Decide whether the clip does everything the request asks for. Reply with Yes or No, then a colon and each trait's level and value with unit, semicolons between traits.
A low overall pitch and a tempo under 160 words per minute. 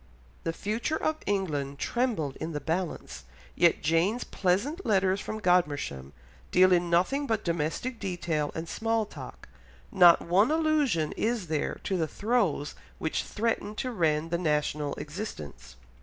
No: medium, 180 Hz; average, 140 wpm